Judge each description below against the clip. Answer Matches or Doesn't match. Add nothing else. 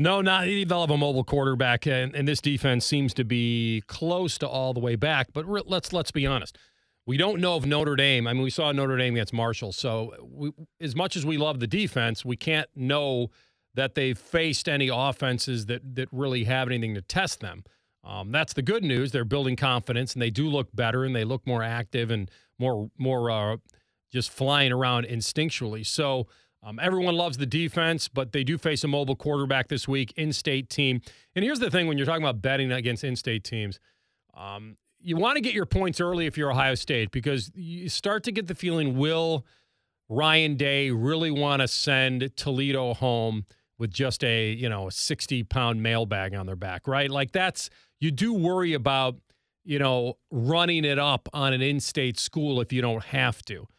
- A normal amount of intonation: Matches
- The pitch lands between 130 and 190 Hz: Matches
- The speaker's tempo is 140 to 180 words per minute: Doesn't match